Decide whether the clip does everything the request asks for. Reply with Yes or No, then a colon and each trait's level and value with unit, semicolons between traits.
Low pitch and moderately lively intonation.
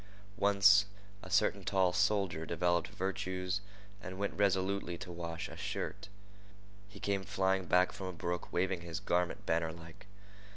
No: very low, 95 Hz; narrow, 2.2 semitones